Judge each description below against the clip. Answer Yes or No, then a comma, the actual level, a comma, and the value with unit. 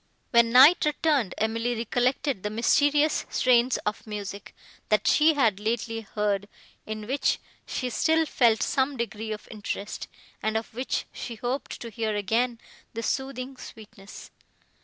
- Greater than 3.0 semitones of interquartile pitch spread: Yes, average, 3.5 semitones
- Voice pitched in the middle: No, high, 230 Hz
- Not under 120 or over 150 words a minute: Yes, average, 140 wpm